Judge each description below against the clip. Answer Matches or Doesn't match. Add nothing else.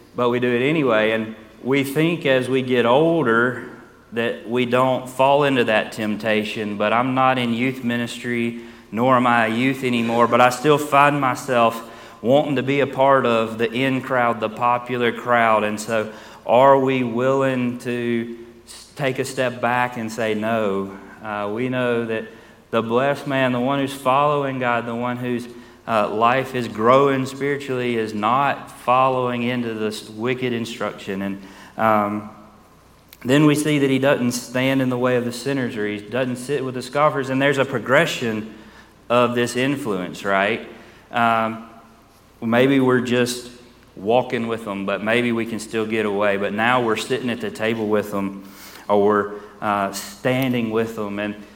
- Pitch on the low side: Matches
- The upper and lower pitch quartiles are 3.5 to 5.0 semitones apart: Doesn't match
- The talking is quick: Doesn't match